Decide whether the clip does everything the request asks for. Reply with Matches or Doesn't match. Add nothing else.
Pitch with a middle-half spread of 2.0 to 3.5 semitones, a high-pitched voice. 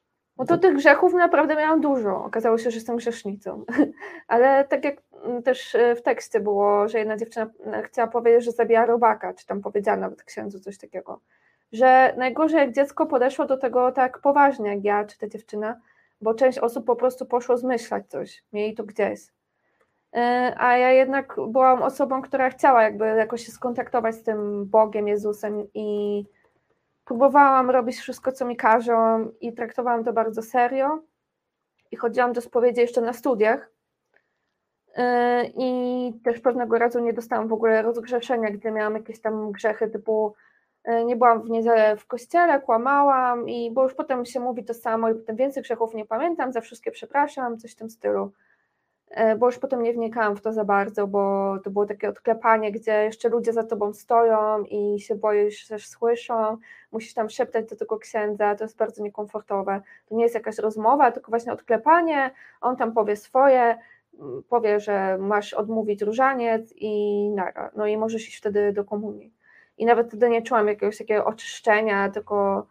Matches